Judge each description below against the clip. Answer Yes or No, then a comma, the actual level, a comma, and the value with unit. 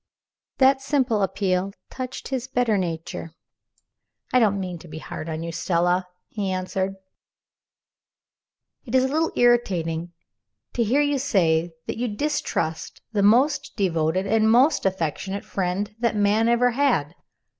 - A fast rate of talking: No, average, 140 wpm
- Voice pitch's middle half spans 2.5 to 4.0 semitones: No, wide, 5.6 semitones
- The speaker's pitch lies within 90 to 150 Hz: No, high, 205 Hz